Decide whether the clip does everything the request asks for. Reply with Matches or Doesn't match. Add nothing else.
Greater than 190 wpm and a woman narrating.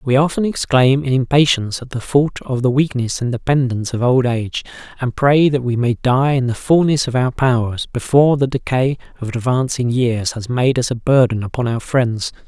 Doesn't match